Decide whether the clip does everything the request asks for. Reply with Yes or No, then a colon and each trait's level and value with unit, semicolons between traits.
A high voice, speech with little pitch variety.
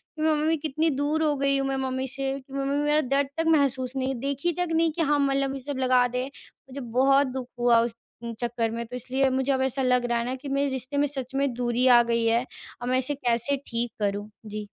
Yes: very high, 265 Hz; narrow, 2.2 semitones